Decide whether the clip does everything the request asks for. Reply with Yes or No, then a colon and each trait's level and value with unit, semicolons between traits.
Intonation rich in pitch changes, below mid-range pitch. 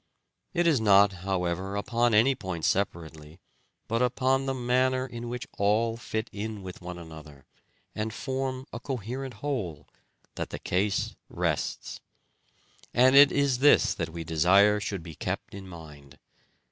Yes: wide, 6.2 semitones; low, 105 Hz